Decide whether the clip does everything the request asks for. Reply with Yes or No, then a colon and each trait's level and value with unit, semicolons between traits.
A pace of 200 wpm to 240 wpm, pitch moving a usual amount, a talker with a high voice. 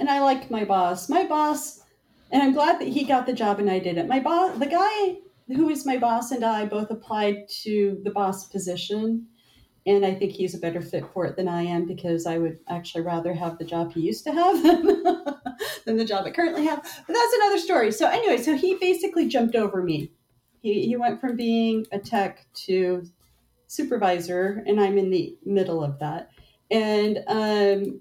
No: fast, 205 wpm; wide, 7.5 semitones; high, 215 Hz